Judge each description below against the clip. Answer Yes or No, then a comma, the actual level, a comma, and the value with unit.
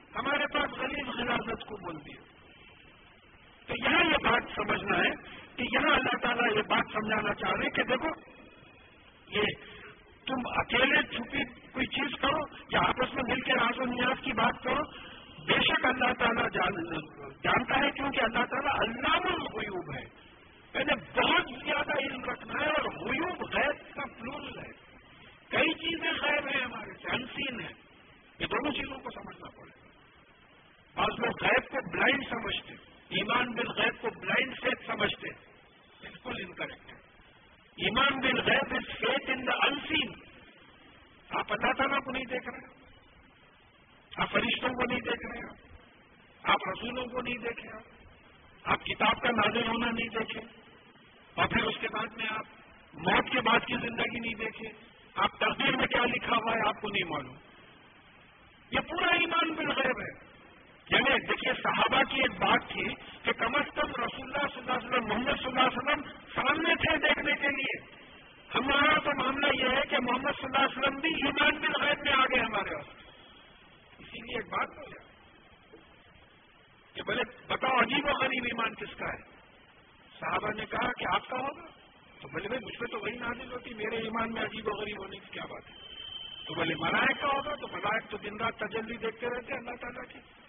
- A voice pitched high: Yes, high, 245 Hz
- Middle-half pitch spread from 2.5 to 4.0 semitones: Yes, average, 3.6 semitones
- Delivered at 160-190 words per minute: Yes, average, 170 wpm